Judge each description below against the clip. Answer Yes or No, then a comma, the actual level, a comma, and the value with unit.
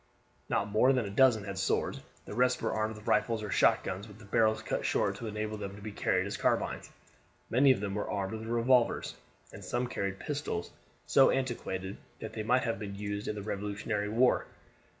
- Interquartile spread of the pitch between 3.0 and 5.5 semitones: No, narrow, 2.6 semitones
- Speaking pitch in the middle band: No, low, 110 Hz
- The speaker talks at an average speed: No, fast, 210 wpm